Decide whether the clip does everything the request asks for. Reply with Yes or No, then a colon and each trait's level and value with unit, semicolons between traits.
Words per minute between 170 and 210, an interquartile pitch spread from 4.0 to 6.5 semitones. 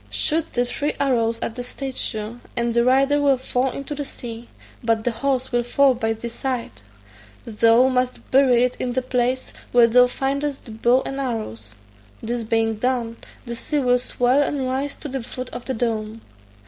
No: average, 185 wpm; narrow, 2.5 semitones